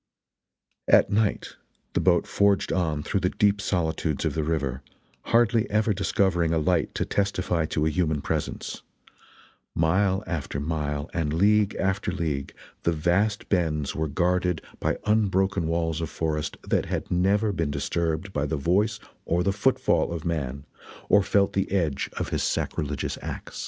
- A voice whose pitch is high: No, very low, 85 Hz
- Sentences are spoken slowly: No, average, 160 wpm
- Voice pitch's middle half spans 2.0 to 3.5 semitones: No, average, 4.0 semitones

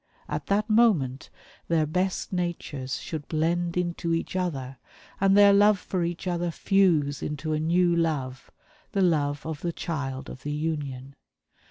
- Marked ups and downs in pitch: No, average, 3.7 semitones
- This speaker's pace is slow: No, average, 155 wpm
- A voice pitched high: No, medium, 165 Hz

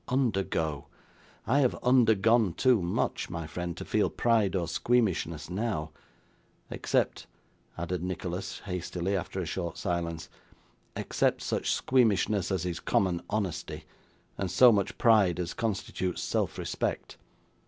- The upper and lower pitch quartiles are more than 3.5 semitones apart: Yes, average, 4.3 semitones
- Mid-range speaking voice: No, very low, 95 Hz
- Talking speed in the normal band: No, slow, 130 wpm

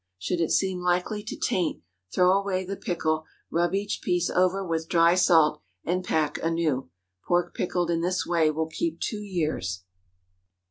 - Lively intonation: No, narrow, 2.4 semitones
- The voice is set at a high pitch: No, medium, 175 Hz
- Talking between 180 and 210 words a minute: No, average, 165 wpm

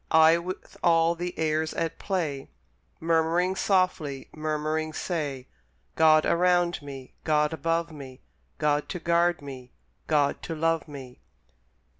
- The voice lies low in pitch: No, medium, 160 Hz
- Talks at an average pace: No, slow, 125 wpm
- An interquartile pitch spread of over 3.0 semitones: No, narrow, 2.5 semitones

